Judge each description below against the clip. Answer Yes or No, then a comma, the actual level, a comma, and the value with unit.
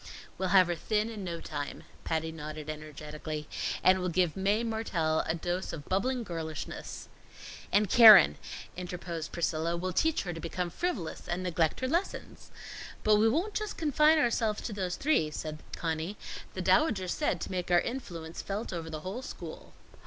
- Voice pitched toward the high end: No, medium, 180 Hz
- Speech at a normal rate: Yes, average, 170 wpm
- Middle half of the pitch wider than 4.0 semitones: Yes, average, 5.1 semitones